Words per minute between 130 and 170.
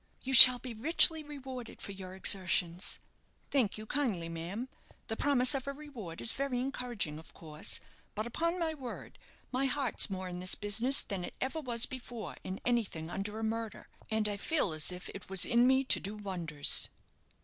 No: average, 185 wpm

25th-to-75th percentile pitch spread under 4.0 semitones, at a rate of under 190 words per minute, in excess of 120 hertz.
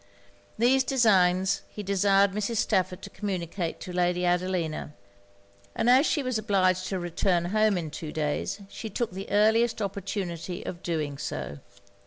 Yes: average, 3.3 semitones; average, 150 wpm; high, 190 Hz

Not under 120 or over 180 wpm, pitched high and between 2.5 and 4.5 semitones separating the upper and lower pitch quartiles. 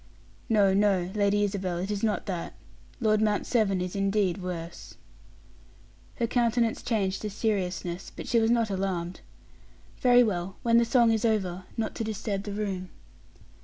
Yes: average, 160 wpm; high, 205 Hz; average, 3.0 semitones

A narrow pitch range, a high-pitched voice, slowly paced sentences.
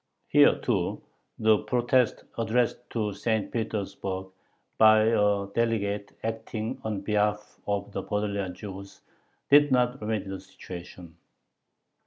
No: narrow, 2.1 semitones; low, 105 Hz; slow, 115 wpm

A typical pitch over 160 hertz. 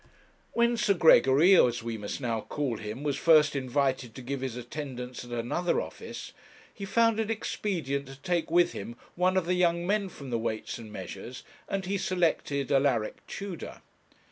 No: medium, 140 Hz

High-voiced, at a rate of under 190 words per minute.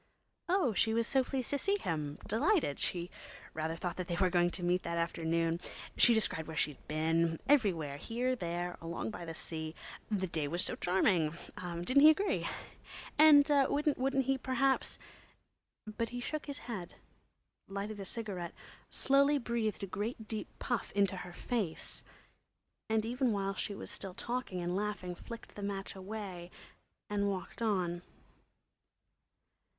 Yes: high, 200 Hz; average, 145 wpm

